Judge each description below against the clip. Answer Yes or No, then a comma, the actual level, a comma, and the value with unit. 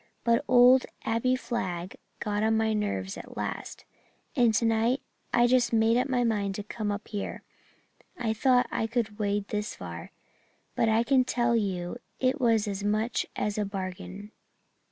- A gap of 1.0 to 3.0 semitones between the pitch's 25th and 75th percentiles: Yes, average, 2.7 semitones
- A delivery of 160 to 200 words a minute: Yes, average, 165 wpm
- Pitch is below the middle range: No, high, 220 Hz